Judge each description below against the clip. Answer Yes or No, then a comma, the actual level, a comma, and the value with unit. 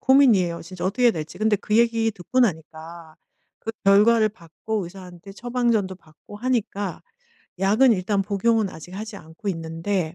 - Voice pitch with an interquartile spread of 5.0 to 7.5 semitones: No, average, 4.4 semitones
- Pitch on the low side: No, high, 200 Hz